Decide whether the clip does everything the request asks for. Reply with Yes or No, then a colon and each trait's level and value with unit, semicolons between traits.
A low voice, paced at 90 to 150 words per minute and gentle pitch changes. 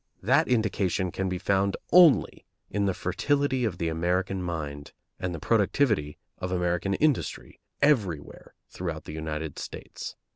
No: very low, 95 Hz; average, 140 wpm; average, 4.9 semitones